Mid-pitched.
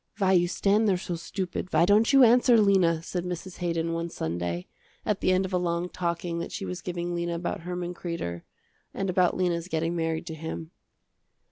Yes: medium, 175 Hz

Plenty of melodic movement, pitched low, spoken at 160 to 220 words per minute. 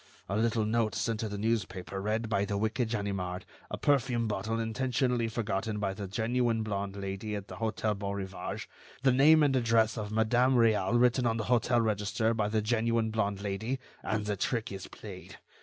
No: narrow, 2.4 semitones; low, 110 Hz; average, 185 wpm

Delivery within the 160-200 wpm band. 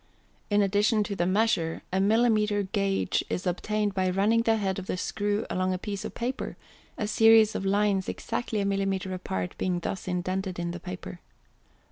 Yes: average, 180 wpm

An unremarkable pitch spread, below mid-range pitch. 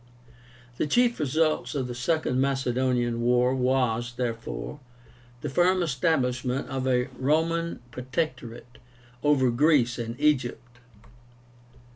Yes: average, 3.5 semitones; low, 130 Hz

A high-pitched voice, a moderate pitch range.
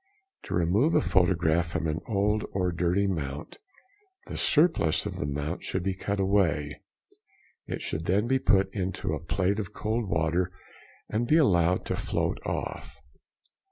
No: very low, 95 Hz; average, 3.7 semitones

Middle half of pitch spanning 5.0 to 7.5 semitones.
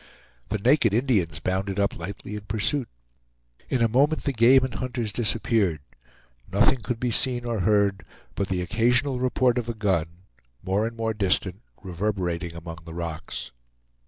No: average, 4.6 semitones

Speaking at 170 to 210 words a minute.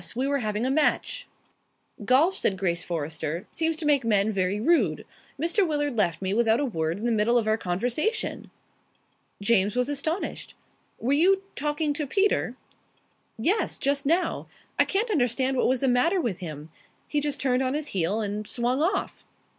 Yes: average, 175 wpm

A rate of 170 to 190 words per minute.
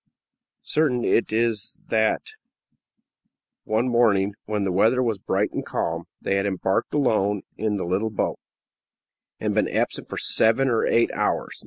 No: average, 150 wpm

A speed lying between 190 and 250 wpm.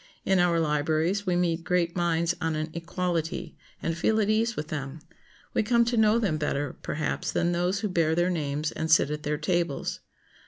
Yes: average, 195 wpm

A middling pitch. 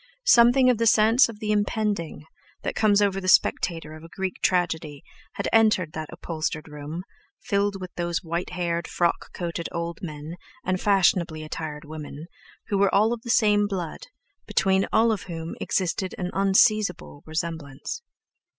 Yes: medium, 180 Hz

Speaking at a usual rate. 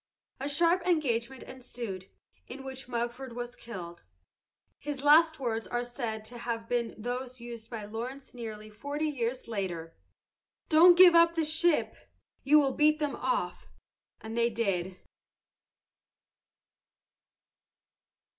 No: slow, 125 wpm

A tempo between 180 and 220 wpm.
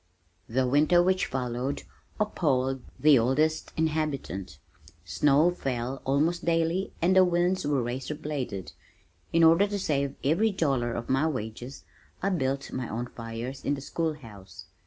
No: average, 145 wpm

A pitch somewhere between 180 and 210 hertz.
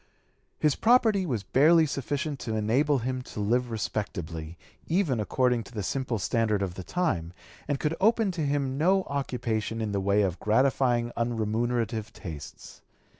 No: low, 120 Hz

